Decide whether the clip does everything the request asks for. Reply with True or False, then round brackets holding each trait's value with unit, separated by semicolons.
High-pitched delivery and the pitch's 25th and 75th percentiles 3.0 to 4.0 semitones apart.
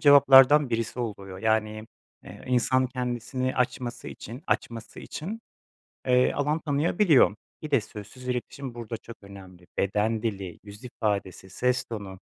False (120 Hz; 3.6 semitones)